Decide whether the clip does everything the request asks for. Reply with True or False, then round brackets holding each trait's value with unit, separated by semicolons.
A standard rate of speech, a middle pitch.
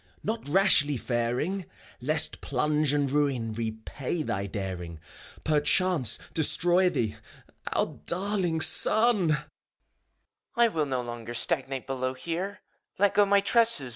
False (130 wpm; 150 Hz)